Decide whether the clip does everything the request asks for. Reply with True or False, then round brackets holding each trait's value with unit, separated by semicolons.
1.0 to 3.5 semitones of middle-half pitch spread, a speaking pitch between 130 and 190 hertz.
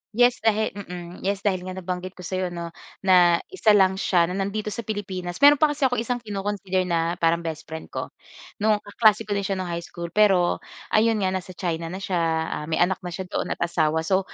True (3.1 semitones; 185 Hz)